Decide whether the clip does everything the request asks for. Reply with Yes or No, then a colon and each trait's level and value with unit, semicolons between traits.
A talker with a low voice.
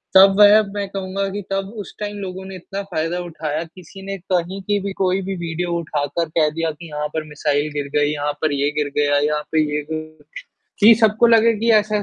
No: medium, 180 Hz